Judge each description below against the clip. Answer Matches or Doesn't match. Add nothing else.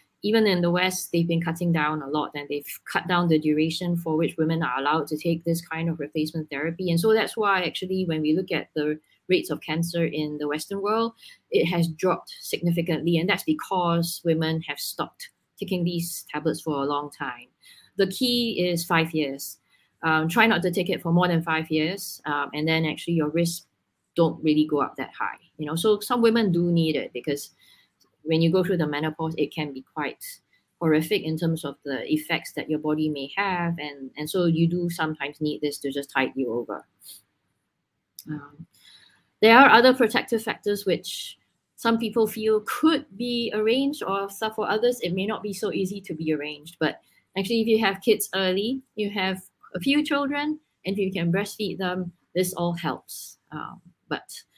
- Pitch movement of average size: Matches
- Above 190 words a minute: Matches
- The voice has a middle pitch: Matches